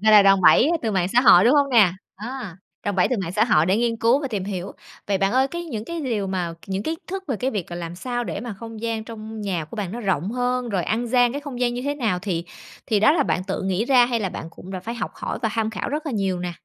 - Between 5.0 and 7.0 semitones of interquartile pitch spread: No, average, 4.4 semitones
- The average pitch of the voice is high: Yes, high, 220 Hz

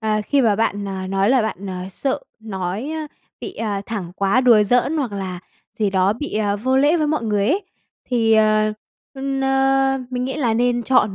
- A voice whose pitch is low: No, high, 225 Hz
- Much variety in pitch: No, average, 4.9 semitones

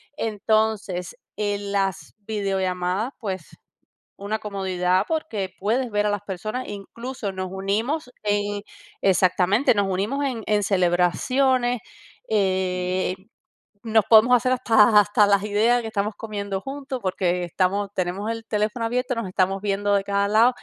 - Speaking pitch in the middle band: No, high, 205 Hz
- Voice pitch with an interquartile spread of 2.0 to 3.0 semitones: Yes, average, 2.7 semitones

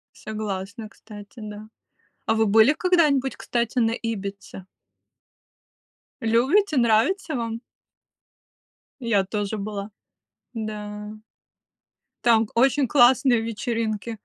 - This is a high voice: Yes, high, 225 Hz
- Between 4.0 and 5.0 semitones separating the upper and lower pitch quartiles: No, average, 2.8 semitones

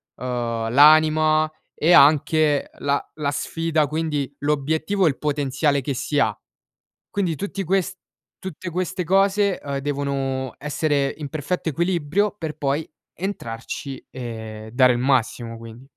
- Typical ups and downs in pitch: Yes, average, 3.4 semitones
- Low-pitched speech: No, medium, 145 Hz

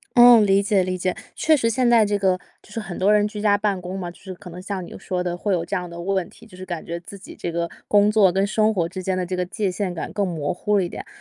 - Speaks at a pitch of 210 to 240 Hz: No, high, 190 Hz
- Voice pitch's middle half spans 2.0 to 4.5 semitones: Yes, narrow, 2.6 semitones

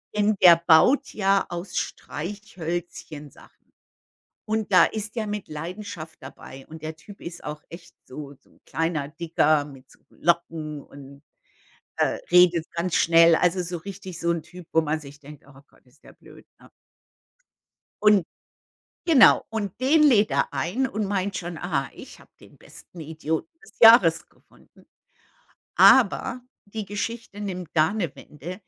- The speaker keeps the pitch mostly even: No, average, 4.6 semitones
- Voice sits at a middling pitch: Yes, medium, 175 Hz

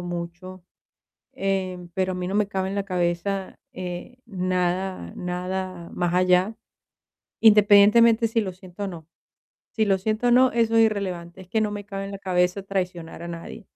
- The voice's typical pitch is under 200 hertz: Yes, high, 190 Hz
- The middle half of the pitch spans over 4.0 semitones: No, narrow, 2.4 semitones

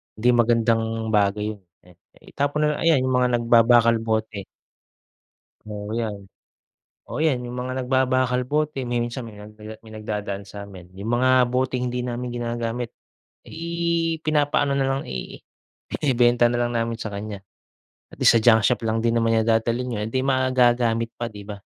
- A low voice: Yes, low, 120 Hz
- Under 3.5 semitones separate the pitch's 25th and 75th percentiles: Yes, narrow, 2.5 semitones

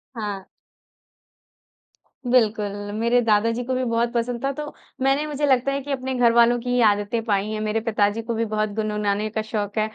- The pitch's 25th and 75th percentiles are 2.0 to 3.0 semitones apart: Yes, narrow, 2.6 semitones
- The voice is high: Yes, high, 230 Hz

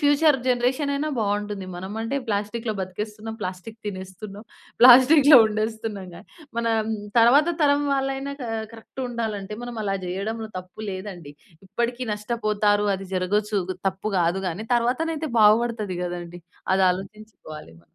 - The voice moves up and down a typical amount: Yes, average, 3.8 semitones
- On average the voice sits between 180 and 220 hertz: Yes, high, 215 Hz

